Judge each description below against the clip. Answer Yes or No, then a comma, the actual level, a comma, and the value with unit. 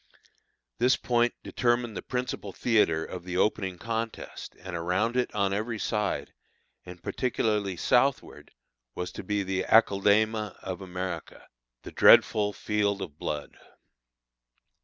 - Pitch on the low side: Yes, low, 105 Hz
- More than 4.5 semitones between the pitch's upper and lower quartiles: No, average, 3.6 semitones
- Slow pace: Yes, slow, 125 wpm